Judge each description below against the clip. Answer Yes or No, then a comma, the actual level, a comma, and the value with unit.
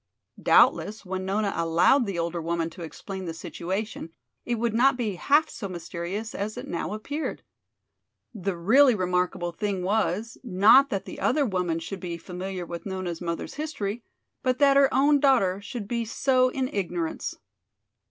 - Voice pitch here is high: Yes, high, 200 Hz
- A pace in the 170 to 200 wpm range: No, average, 160 wpm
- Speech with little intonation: No, wide, 5.5 semitones